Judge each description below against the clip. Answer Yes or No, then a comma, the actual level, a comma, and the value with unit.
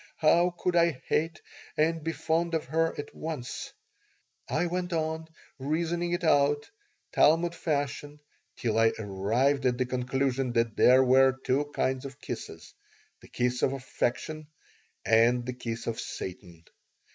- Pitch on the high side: No, medium, 140 Hz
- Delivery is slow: No, average, 145 wpm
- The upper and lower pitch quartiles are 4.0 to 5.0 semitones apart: Yes, average, 4.6 semitones